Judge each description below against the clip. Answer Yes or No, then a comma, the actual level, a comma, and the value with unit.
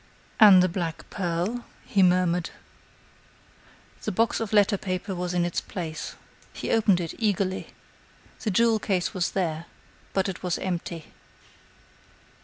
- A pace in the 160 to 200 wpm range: No, slow, 135 wpm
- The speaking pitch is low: No, medium, 185 Hz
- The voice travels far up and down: No, average, 2.8 semitones